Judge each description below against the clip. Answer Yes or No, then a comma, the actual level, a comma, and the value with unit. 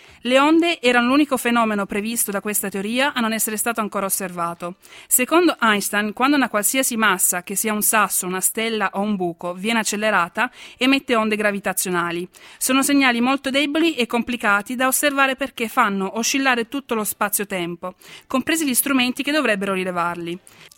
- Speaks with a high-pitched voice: Yes, high, 225 Hz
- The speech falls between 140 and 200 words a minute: Yes, average, 160 wpm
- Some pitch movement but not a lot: Yes, average, 4.6 semitones